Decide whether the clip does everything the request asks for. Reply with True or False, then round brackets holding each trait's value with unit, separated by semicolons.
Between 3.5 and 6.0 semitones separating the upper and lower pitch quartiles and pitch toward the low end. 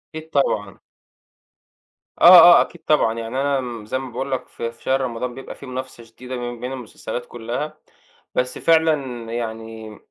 False (2.8 semitones; 125 Hz)